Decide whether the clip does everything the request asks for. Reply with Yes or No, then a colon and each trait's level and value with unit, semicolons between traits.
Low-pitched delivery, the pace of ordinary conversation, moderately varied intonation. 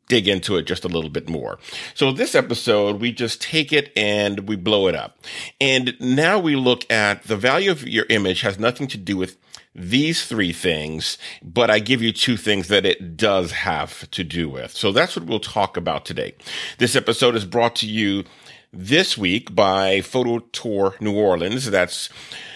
Yes: low, 110 Hz; average, 190 wpm; average, 4.0 semitones